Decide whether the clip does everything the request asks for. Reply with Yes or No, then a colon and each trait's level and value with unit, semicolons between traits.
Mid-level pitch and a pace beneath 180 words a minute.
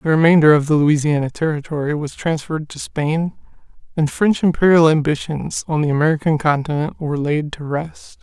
Yes: medium, 155 Hz; average, 160 wpm